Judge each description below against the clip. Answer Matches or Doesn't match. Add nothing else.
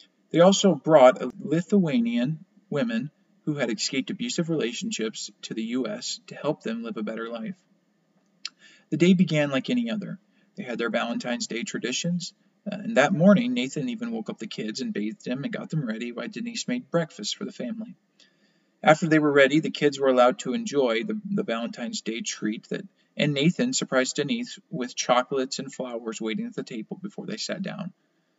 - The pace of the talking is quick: Doesn't match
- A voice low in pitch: Doesn't match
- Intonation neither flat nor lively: Doesn't match